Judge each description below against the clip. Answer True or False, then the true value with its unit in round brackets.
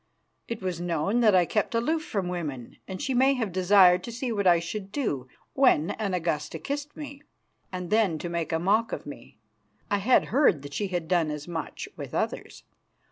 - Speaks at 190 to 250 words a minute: True (200 wpm)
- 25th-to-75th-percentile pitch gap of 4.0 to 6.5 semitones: True (5.5 semitones)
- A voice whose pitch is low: False (185 Hz)